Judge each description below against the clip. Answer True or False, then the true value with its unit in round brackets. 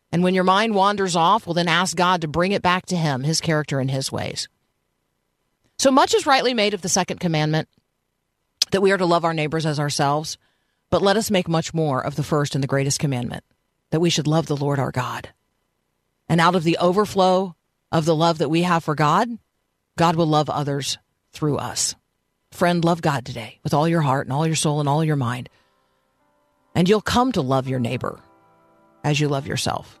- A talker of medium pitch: True (155 Hz)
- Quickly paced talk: True (210 wpm)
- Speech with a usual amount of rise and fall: True (4.6 semitones)